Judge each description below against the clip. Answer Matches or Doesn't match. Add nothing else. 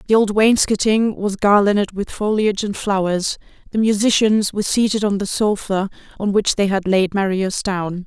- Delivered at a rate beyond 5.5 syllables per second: Doesn't match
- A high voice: Matches